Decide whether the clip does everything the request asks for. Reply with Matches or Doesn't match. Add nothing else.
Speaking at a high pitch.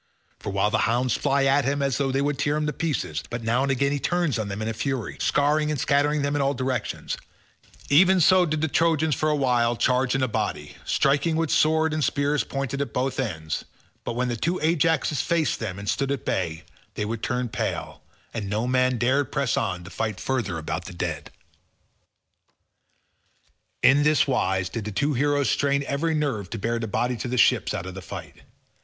Doesn't match